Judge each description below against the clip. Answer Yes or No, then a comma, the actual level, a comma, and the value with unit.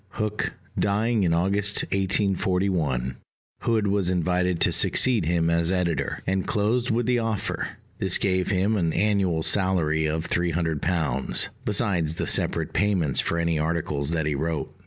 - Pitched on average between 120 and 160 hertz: No, very low, 90 Hz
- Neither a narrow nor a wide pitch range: Yes, average, 3.7 semitones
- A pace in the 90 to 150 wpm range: Yes, average, 145 wpm